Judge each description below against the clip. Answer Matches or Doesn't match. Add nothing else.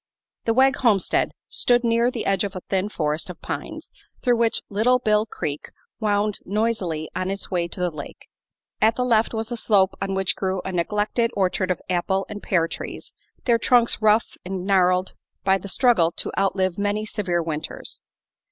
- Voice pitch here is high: Matches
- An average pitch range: Matches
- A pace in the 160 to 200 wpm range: Matches